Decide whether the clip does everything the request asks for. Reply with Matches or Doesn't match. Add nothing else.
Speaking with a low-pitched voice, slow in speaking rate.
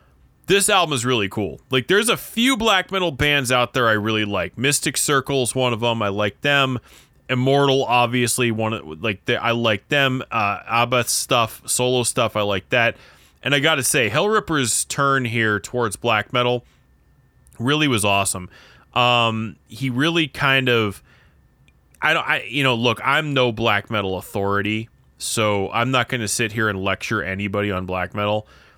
Doesn't match